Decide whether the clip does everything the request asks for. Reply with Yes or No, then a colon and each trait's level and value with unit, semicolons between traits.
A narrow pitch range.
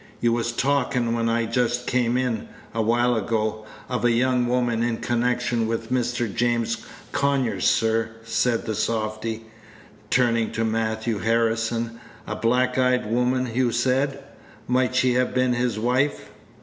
Yes: narrow, 1.7 semitones